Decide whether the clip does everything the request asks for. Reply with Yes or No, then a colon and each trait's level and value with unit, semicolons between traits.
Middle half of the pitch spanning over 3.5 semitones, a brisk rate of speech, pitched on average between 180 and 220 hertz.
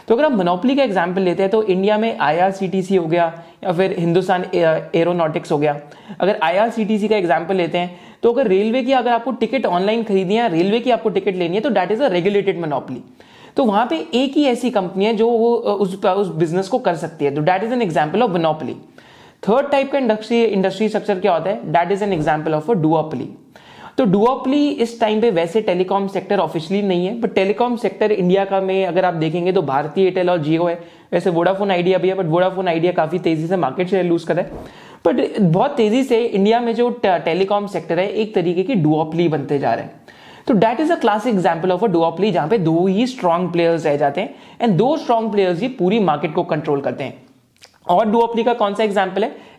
Yes: average, 4.5 semitones; fast, 215 wpm; high, 190 Hz